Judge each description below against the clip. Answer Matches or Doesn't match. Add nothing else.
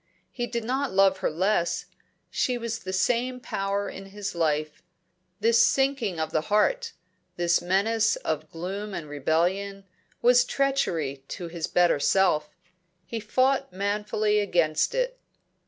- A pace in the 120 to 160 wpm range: Matches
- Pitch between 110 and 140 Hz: Doesn't match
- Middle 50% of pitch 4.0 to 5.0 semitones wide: Doesn't match